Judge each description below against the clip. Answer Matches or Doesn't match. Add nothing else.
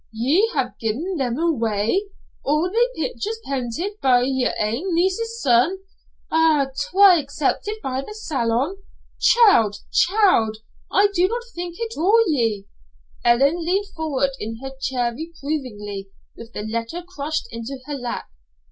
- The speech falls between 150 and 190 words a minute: Doesn't match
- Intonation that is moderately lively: Doesn't match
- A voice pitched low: Doesn't match